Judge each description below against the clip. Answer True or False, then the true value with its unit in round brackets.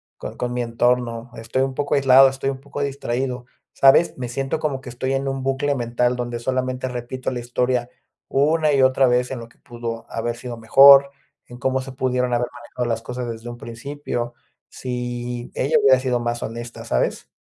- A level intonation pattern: True (2.0 semitones)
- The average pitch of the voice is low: True (125 Hz)